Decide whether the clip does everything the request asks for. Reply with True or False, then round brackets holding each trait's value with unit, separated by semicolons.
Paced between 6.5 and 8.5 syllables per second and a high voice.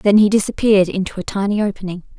True (6.9 syllables/s; 200 Hz)